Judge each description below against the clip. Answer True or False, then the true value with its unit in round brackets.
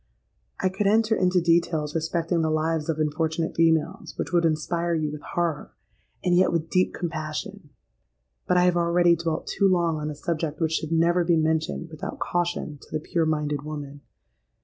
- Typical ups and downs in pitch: False (2.0 semitones)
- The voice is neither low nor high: True (165 Hz)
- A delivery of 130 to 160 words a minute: False (175 wpm)